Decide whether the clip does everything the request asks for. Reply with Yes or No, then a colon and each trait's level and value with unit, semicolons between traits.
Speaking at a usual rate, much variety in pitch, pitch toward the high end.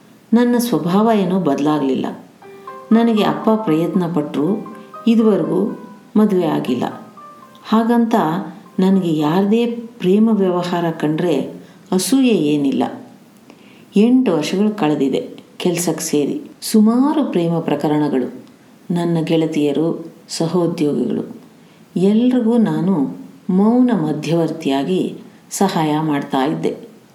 Yes: average, 80 wpm; wide, 6.1 semitones; high, 195 Hz